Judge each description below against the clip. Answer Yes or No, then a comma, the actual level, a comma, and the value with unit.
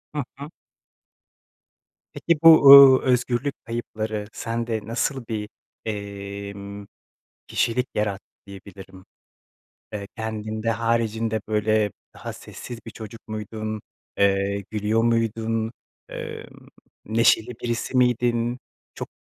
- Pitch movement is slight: Yes, narrow, 2.0 semitones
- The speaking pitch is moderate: No, low, 110 Hz